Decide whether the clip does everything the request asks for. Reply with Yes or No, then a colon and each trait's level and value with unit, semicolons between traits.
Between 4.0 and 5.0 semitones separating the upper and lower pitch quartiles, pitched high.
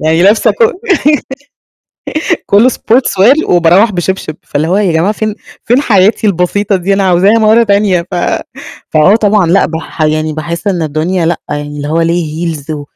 No: average, 4.3 semitones; medium, 180 Hz